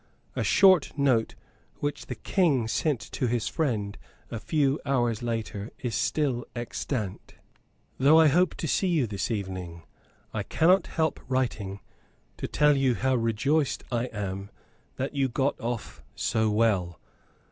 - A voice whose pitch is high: No, low, 120 Hz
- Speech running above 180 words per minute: No, average, 145 wpm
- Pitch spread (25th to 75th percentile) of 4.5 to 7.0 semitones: Yes, average, 4.9 semitones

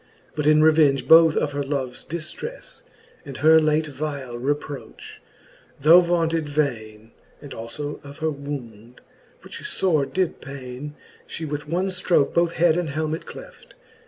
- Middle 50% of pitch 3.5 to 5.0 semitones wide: No, average, 2.9 semitones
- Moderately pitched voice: Yes, medium, 150 Hz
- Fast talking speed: No, average, 145 wpm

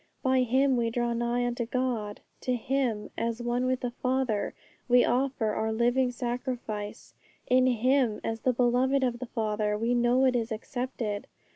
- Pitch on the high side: Yes, high, 245 Hz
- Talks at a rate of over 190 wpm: No, average, 165 wpm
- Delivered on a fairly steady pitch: Yes, narrow, 2.1 semitones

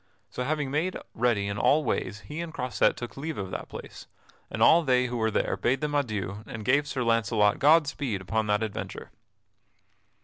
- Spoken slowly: No, average, 195 wpm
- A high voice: No, low, 125 Hz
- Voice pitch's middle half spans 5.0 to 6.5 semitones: Yes, wide, 5.6 semitones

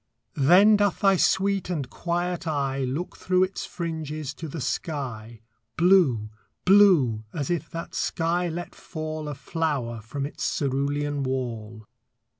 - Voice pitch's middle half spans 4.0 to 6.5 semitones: Yes, average, 4.8 semitones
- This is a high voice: No, medium, 155 Hz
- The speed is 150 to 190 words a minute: No, slow, 135 wpm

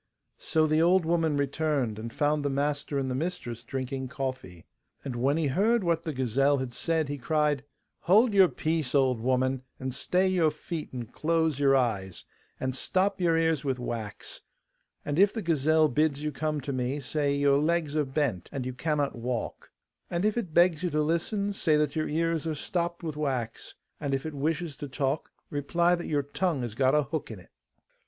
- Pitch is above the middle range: No, medium, 150 Hz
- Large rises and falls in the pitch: No, average, 3.8 semitones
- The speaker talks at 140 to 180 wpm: No, average, 195 wpm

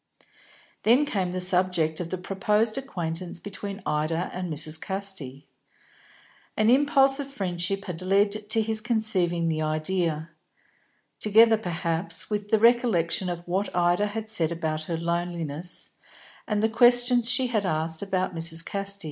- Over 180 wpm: No, average, 145 wpm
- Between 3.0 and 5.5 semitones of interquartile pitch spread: Yes, average, 4.4 semitones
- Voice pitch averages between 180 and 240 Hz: Yes, medium, 185 Hz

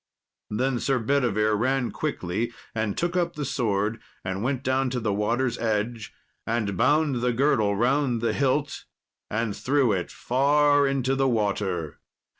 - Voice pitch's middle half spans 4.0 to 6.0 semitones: Yes, average, 4.3 semitones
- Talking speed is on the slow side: No, average, 150 wpm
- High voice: No, low, 120 Hz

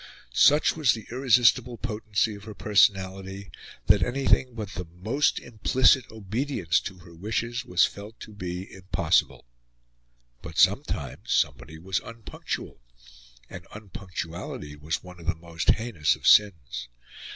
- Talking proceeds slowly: Yes, slow, 130 wpm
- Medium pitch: No, low, 100 Hz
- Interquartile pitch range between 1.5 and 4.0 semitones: No, average, 4.7 semitones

